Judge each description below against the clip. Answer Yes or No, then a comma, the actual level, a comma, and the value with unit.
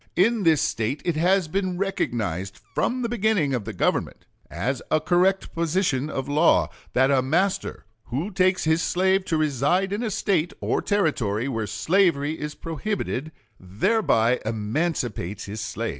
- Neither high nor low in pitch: Yes, medium, 155 Hz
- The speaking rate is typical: Yes, average, 155 wpm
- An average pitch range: No, wide, 7.5 semitones